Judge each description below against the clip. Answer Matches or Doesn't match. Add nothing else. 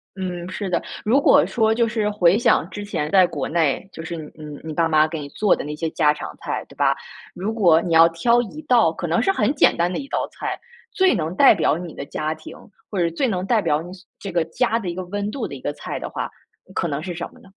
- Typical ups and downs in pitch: Matches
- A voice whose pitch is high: Doesn't match